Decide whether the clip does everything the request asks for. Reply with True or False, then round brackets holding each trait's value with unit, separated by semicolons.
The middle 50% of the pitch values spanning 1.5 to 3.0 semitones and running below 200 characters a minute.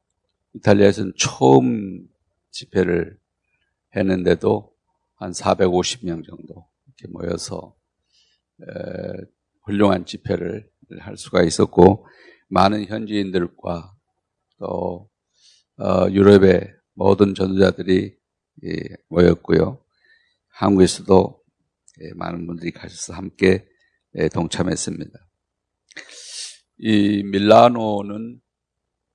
True (2.5 semitones; 175 characters per minute)